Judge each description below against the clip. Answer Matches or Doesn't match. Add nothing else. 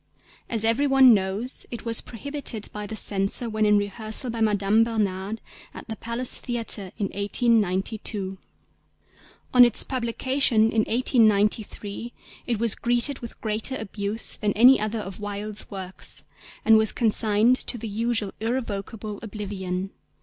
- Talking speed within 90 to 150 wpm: Matches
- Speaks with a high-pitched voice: Matches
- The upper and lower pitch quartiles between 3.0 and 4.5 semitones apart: Doesn't match